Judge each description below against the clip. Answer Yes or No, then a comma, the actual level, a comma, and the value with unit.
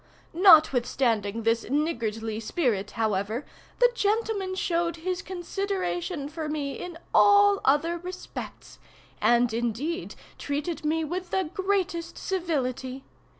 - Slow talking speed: Yes, slow, 110 wpm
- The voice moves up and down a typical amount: No, wide, 7.0 semitones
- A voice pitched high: Yes, very high, 320 Hz